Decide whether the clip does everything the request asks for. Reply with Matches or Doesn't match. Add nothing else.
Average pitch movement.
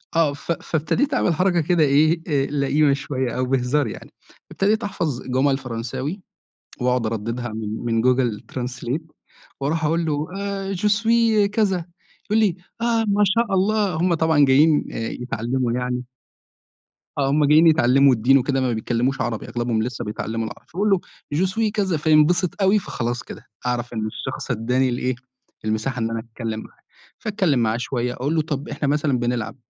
Doesn't match